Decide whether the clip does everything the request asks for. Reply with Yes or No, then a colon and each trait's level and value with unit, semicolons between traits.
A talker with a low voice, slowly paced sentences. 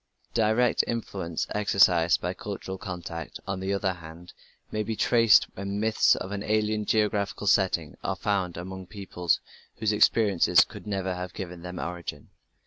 No: very low, 95 Hz; average, 155 wpm